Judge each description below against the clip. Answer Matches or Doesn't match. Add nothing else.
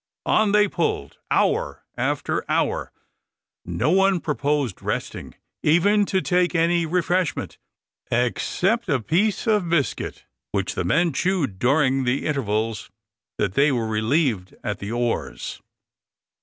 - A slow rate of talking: Matches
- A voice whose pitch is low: Doesn't match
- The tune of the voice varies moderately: Doesn't match